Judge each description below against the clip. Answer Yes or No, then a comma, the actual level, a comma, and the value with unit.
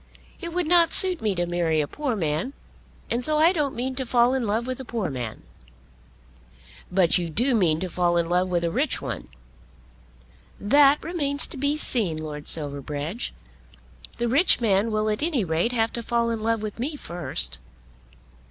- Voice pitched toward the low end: No, high, 225 Hz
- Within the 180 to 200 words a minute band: Yes, average, 185 wpm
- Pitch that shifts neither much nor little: No, wide, 7.6 semitones